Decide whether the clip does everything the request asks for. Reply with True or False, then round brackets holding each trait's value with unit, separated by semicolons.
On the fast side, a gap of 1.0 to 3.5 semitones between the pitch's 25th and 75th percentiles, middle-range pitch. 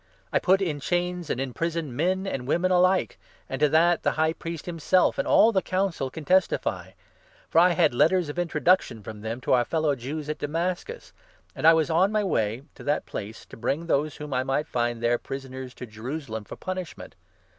False (210 wpm; 5.2 semitones; 155 Hz)